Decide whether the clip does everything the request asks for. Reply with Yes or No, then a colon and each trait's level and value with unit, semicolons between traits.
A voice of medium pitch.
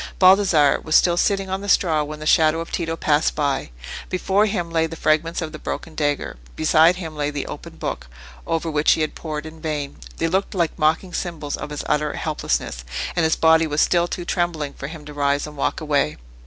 Yes: medium, 160 Hz